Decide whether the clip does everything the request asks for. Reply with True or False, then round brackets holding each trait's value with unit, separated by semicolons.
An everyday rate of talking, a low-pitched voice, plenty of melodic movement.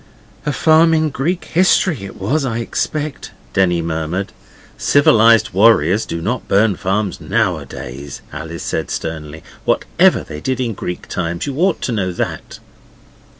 True (145 wpm; 105 Hz; 8.4 semitones)